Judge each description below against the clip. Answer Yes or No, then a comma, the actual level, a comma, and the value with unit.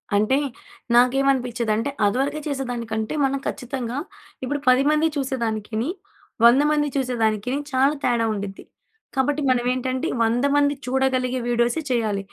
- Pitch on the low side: No, very high, 250 Hz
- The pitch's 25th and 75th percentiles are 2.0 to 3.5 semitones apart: Yes, average, 2.8 semitones